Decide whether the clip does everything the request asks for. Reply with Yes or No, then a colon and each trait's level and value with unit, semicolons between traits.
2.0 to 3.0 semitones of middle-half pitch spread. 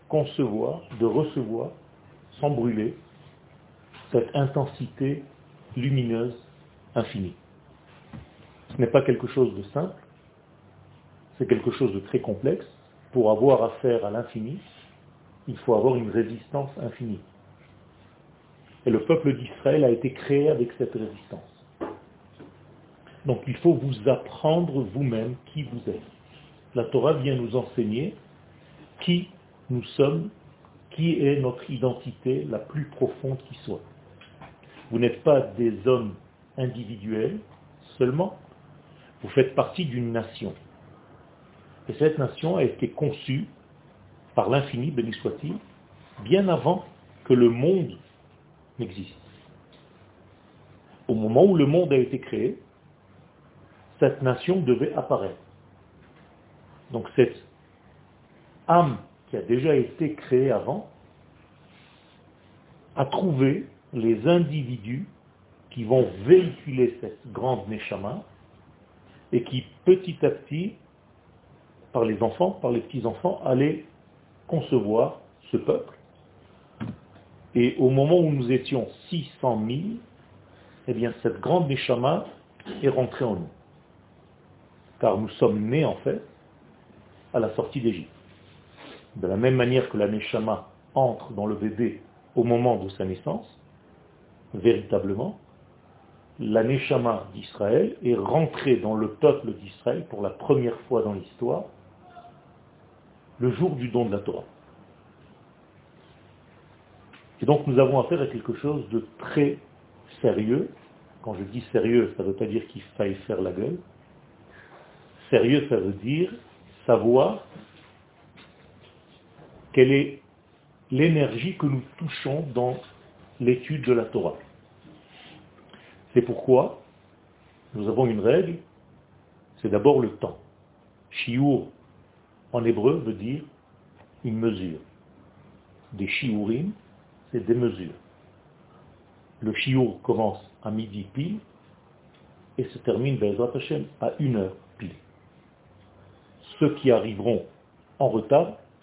No: average, 4.0 semitones